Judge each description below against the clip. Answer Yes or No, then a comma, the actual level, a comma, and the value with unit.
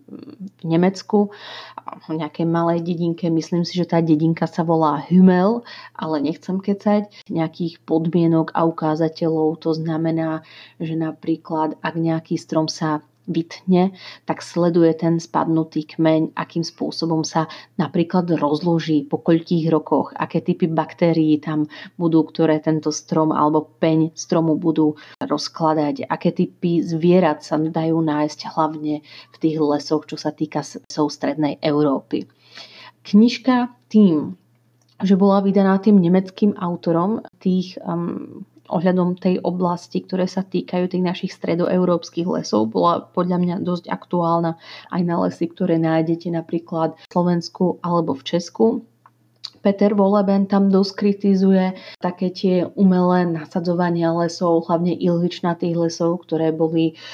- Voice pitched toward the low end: No, medium, 170 Hz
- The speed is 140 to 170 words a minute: No, average, 130 wpm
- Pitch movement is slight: Yes, narrow, 2.3 semitones